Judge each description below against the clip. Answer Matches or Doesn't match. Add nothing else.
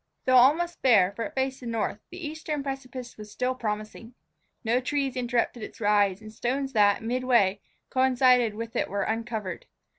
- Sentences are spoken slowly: Doesn't match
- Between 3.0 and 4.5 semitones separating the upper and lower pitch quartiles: Matches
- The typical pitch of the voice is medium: Doesn't match